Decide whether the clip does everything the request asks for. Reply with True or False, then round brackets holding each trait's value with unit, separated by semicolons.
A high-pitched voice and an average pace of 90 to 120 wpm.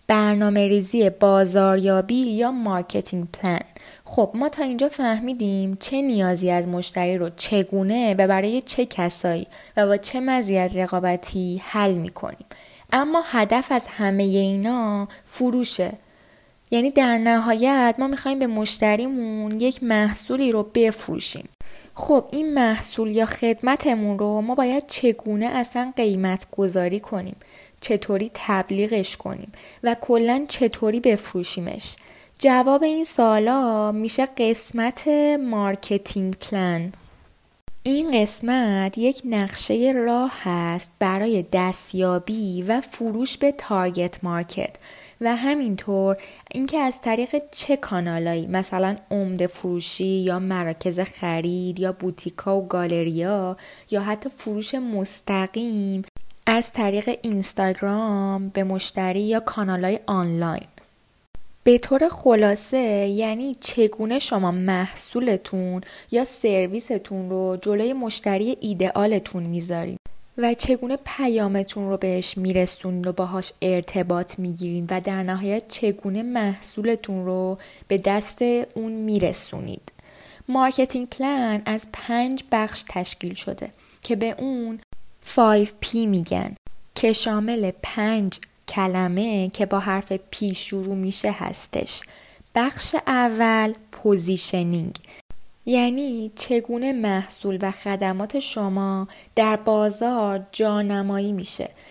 True (210 Hz; 110 wpm)